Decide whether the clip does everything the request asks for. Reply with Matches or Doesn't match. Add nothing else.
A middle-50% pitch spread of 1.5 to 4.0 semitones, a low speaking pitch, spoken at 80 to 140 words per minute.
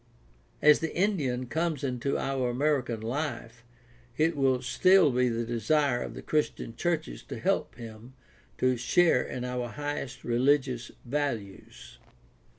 Matches